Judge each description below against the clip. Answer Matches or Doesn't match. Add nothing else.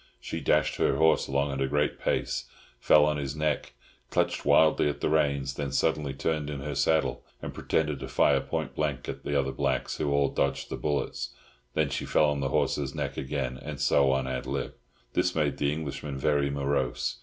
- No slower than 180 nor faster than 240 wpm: Matches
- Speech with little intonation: Matches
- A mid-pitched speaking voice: Doesn't match